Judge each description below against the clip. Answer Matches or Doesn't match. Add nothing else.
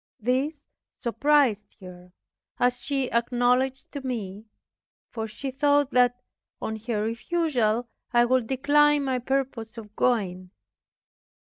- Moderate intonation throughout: Matches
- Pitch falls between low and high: Doesn't match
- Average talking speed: Doesn't match